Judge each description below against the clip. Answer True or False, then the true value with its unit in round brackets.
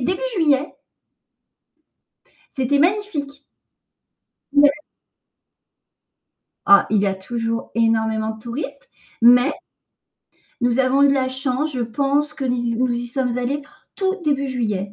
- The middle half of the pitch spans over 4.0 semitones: False (3.5 semitones)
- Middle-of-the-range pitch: False (255 Hz)